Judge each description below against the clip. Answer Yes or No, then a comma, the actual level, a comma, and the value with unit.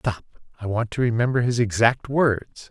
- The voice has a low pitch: Yes, low, 115 Hz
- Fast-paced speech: No, average, 180 wpm